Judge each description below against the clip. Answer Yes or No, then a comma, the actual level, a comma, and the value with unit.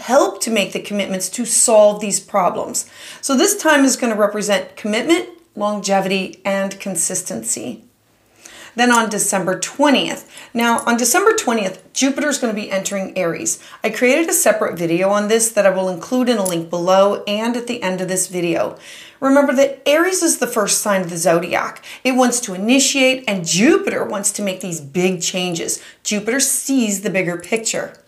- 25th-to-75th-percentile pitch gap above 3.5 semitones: Yes, average, 5.0 semitones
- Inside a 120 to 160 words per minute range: No, average, 180 wpm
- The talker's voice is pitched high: Yes, high, 210 Hz